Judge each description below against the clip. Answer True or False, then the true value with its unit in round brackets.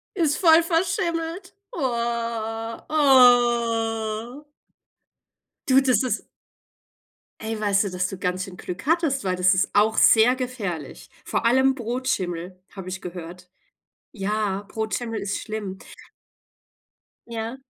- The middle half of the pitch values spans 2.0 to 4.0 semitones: False (5.0 semitones)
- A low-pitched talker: False (225 Hz)